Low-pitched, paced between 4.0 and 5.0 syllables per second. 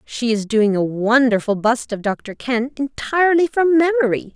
No: very high, 250 Hz; 4.5 syllables/s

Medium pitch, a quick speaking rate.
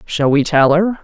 Yes: medium, 165 Hz; fast, 230 wpm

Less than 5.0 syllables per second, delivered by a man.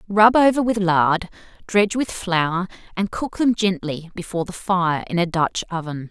No: 4.7 syllables/s; female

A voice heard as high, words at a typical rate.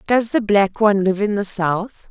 No: high, 205 Hz; fast, 230 wpm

